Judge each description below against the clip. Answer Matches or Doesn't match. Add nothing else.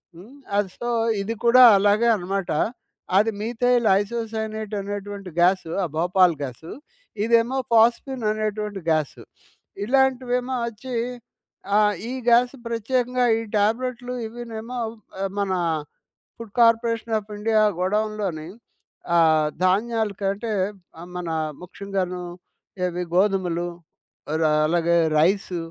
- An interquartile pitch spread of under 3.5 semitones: Doesn't match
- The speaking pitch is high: Matches